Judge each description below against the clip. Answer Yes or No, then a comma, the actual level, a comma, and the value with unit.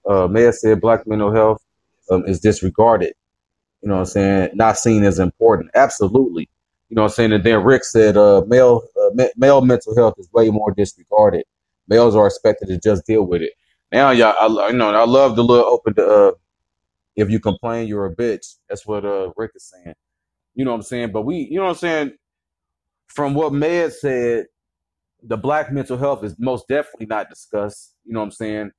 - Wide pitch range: No, average, 4.0 semitones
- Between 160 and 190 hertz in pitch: No, low, 110 Hz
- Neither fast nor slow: No, fast, 210 wpm